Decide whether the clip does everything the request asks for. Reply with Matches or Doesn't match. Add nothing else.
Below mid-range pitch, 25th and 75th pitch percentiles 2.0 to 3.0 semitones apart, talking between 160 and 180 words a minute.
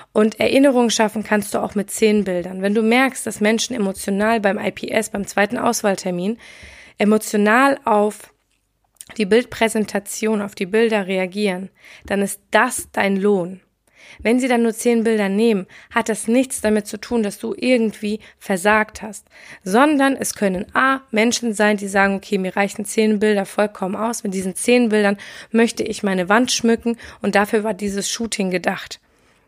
Doesn't match